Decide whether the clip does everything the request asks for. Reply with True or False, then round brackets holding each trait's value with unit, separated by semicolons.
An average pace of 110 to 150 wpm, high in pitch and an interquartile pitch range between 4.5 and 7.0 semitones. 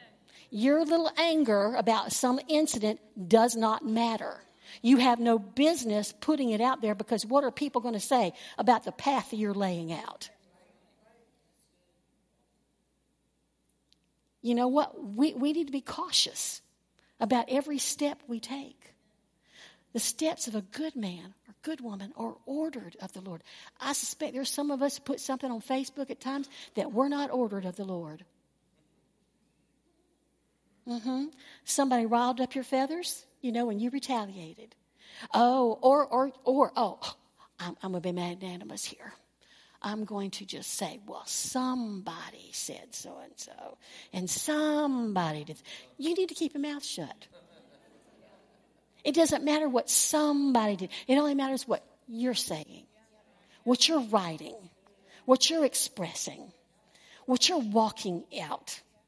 True (145 wpm; 250 Hz; 4.9 semitones)